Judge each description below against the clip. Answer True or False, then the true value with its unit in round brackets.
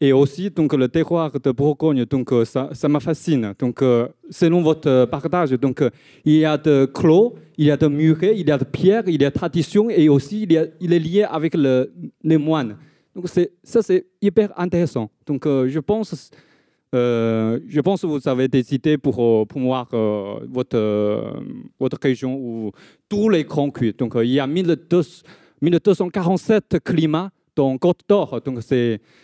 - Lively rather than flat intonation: False (4.9 semitones)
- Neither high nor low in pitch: True (150 Hz)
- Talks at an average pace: True (185 wpm)